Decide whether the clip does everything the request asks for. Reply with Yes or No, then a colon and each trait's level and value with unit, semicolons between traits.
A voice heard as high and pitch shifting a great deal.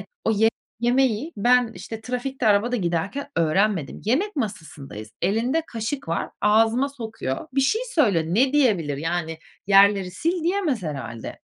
Yes: high, 220 Hz; wide, 7.6 semitones